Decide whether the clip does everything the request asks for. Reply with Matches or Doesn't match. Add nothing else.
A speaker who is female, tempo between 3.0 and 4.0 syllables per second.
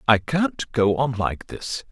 Doesn't match